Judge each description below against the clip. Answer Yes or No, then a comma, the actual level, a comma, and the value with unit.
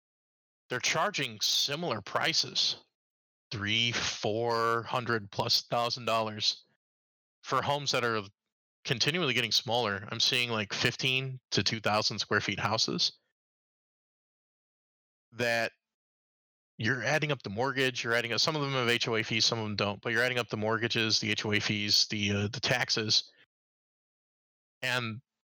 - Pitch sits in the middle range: No, low, 115 Hz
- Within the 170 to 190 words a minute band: No, average, 140 wpm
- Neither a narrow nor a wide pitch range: Yes, average, 3.0 semitones